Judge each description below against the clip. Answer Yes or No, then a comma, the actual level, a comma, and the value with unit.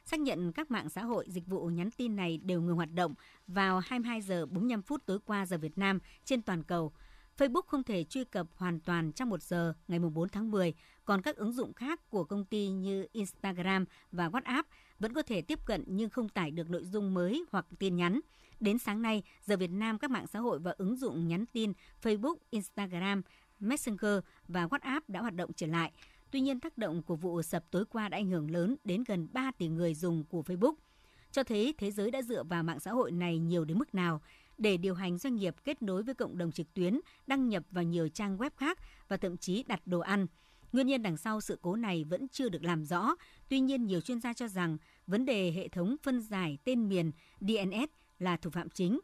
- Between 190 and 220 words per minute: No, average, 230 wpm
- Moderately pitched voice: No, high, 195 Hz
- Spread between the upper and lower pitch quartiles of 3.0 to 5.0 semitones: No, wide, 5.4 semitones